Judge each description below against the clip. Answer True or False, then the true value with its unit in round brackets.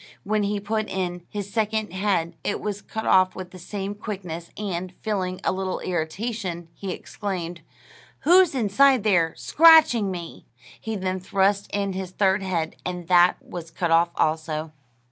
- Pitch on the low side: False (190 Hz)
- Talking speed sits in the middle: True (160 wpm)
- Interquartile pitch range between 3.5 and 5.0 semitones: False (3.0 semitones)